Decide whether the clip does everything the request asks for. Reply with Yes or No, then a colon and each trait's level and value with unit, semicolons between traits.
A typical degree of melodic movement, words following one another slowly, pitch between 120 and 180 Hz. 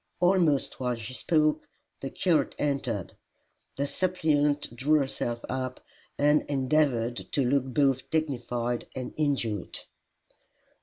Yes: average, 3.7 semitones; slow, 110 wpm; medium, 140 Hz